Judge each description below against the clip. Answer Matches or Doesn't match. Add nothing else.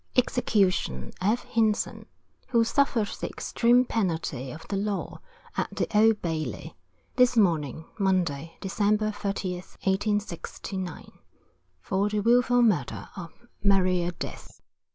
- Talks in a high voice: Matches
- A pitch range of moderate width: Matches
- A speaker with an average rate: Doesn't match